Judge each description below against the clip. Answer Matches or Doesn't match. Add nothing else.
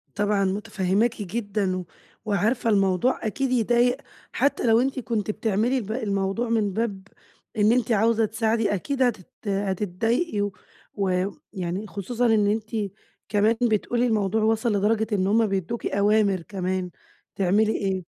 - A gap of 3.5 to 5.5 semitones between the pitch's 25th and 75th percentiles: Doesn't match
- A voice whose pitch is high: Matches